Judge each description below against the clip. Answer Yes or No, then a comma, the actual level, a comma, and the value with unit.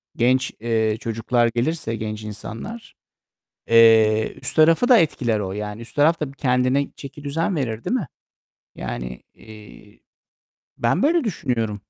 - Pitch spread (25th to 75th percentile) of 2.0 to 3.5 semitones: No, average, 5.1 semitones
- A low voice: Yes, low, 120 Hz